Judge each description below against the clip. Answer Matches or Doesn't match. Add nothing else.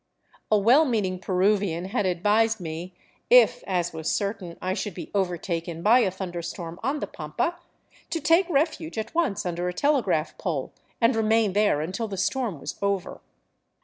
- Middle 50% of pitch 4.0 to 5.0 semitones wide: Matches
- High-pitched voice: Matches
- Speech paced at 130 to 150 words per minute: Doesn't match